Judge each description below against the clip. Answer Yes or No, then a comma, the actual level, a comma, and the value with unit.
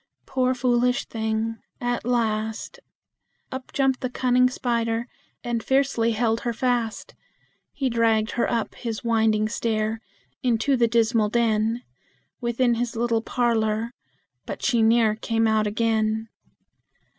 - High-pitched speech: Yes, high, 230 Hz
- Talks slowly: Yes, slow, 125 wpm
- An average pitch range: No, narrow, 1.7 semitones